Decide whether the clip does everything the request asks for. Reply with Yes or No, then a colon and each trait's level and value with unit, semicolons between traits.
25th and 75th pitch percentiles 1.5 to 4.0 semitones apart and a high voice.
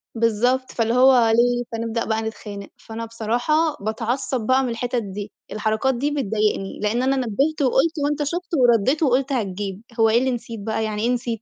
Yes: average, 3.1 semitones; high, 235 Hz